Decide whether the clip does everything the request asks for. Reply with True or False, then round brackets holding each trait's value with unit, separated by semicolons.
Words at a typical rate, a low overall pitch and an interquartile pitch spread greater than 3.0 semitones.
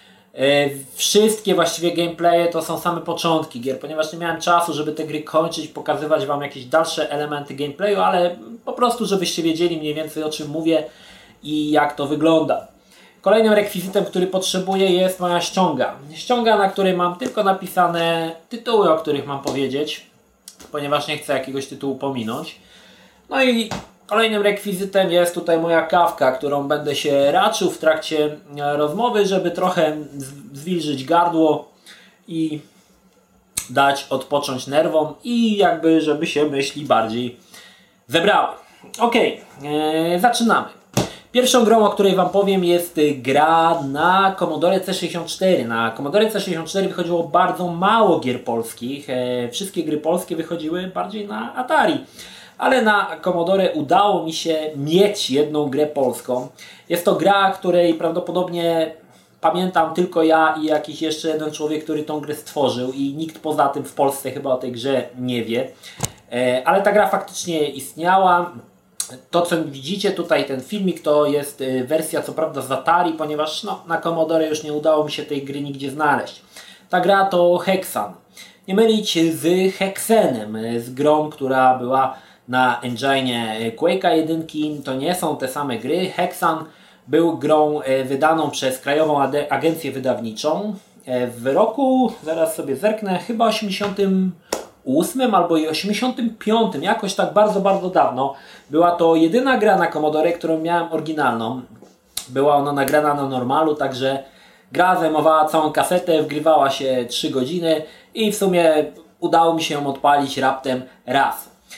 False (145 wpm; 160 Hz; 4.1 semitones)